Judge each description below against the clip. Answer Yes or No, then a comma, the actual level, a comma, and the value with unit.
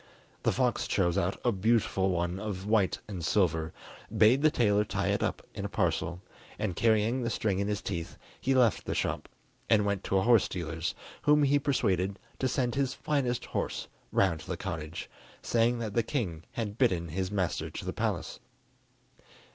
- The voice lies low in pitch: Yes, low, 105 Hz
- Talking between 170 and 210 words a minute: Yes, average, 185 wpm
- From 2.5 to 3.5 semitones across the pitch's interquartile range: No, average, 4.6 semitones